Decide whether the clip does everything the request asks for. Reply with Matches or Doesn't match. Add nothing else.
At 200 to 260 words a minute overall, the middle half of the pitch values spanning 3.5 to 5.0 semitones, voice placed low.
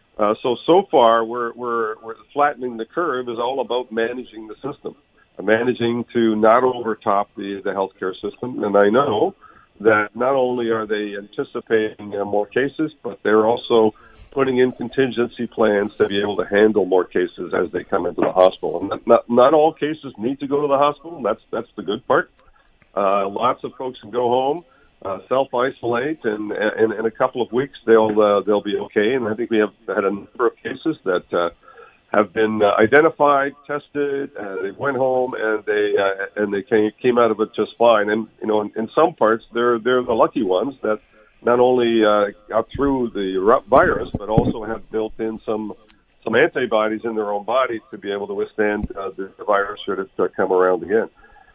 Doesn't match